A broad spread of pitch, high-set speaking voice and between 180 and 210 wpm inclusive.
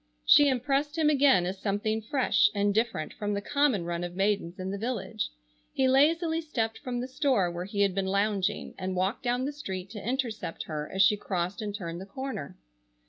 Yes: wide, 5.8 semitones; high, 210 Hz; average, 200 wpm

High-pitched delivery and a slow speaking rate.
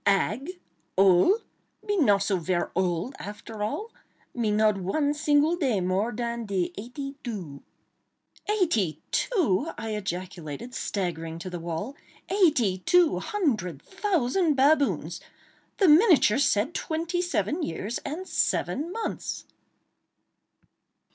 Yes: high, 235 Hz; slow, 110 wpm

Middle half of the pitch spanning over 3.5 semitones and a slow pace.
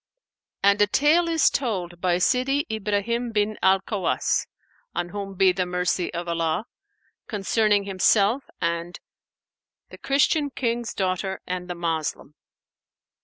Yes: average, 4.6 semitones; slow, 120 wpm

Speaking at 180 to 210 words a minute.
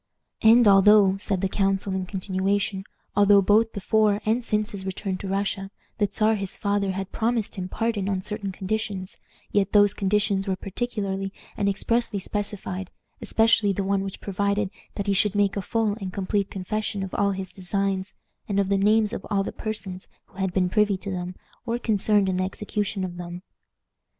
Yes: average, 185 wpm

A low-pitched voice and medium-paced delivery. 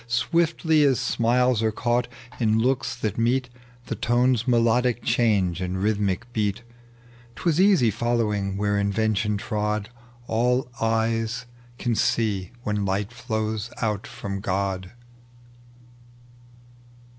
No: low, 115 Hz; slow, 115 wpm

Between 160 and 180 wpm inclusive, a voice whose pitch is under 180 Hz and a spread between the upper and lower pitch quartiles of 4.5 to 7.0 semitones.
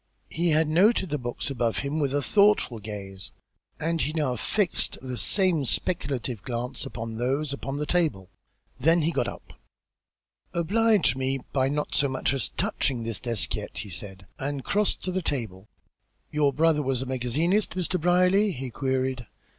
Yes: average, 170 wpm; medium, 140 Hz; wide, 5.4 semitones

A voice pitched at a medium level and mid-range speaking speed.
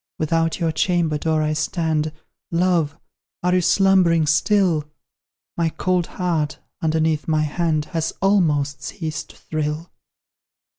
No: medium, 160 Hz; slow, 120 wpm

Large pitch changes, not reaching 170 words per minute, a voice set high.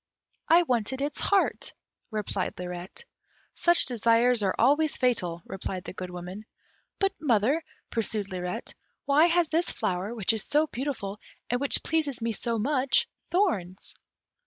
Yes: wide, 7.2 semitones; average, 140 wpm; high, 235 Hz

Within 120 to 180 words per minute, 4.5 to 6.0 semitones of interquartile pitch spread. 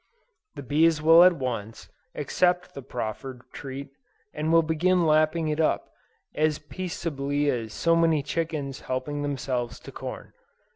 No: average, 140 wpm; average, 3.5 semitones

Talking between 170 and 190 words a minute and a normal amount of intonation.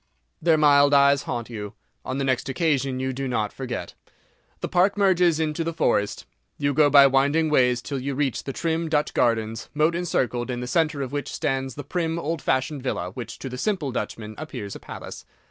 No: average, 200 wpm; average, 3.7 semitones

